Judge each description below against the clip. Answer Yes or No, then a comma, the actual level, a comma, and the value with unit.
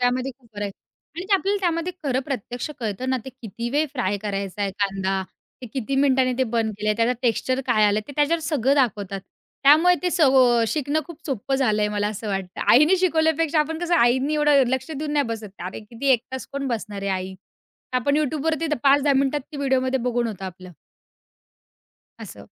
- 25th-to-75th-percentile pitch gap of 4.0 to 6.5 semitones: Yes, wide, 5.5 semitones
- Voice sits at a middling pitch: No, very high, 260 Hz